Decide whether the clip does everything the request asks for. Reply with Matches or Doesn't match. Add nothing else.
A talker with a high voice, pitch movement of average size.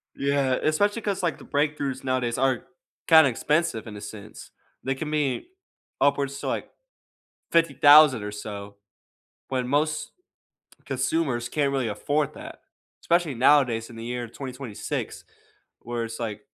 Doesn't match